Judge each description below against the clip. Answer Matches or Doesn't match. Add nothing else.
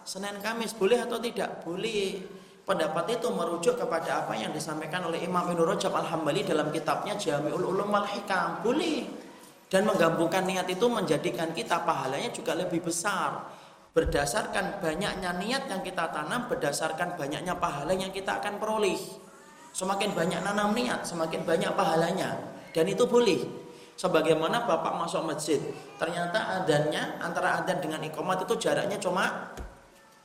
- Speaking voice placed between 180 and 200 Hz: Matches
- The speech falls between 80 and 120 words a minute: Doesn't match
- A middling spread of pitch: Matches